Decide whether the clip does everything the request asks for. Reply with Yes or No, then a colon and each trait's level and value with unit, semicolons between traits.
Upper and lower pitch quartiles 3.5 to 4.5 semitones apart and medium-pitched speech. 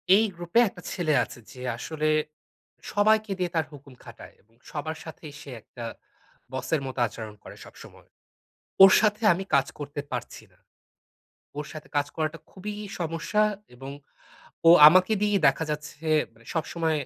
Yes: average, 4.2 semitones; medium, 160 Hz